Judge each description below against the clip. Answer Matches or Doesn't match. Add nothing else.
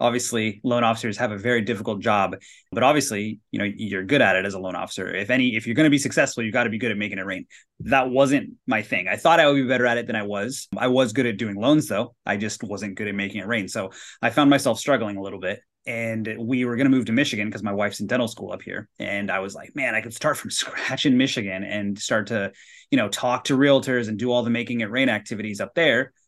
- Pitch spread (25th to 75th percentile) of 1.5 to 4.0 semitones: Matches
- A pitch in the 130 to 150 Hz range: Doesn't match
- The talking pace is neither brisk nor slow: Doesn't match